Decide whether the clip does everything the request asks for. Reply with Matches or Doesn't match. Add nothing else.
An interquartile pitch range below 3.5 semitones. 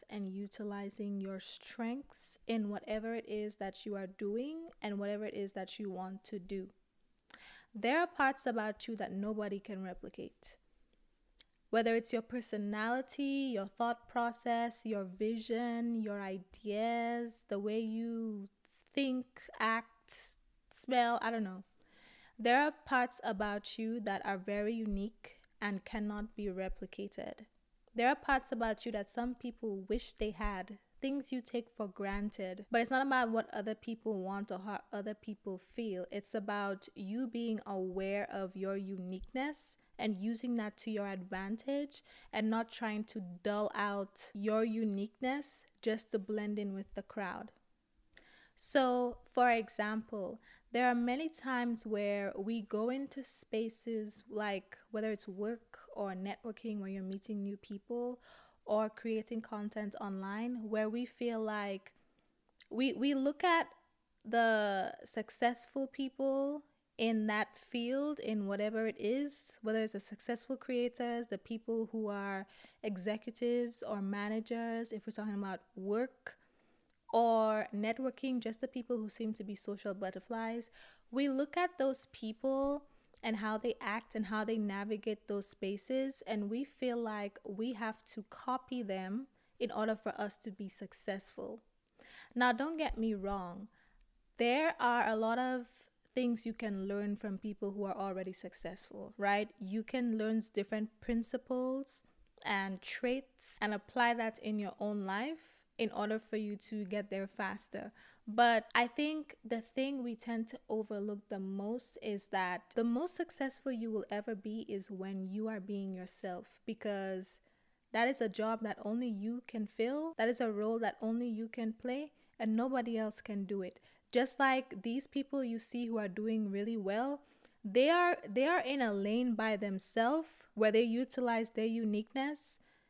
Matches